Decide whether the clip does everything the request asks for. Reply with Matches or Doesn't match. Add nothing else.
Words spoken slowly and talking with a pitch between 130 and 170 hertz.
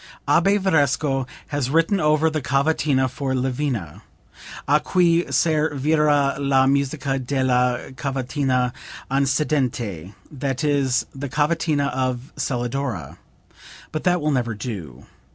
Matches